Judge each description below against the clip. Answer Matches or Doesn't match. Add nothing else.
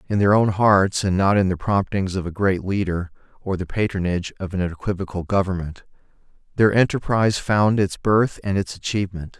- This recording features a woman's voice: Doesn't match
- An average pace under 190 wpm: Matches